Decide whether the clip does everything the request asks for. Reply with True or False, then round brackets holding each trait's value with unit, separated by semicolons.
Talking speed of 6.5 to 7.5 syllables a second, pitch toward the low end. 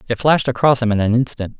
True (7.1 syllables/s; 120 Hz)